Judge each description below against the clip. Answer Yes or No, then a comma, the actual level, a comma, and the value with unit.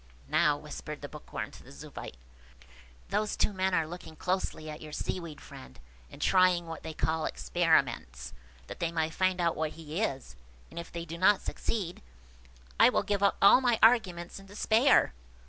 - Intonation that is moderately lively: Yes, average, 3.6 semitones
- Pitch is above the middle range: No, medium, 170 Hz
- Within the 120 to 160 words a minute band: No, average, 180 wpm